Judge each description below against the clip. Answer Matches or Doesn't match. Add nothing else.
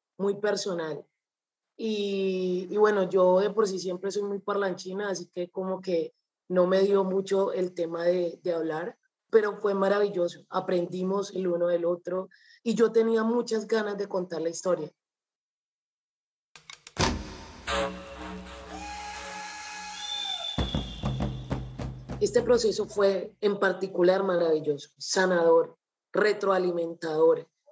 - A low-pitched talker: Doesn't match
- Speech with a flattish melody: Doesn't match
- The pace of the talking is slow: Matches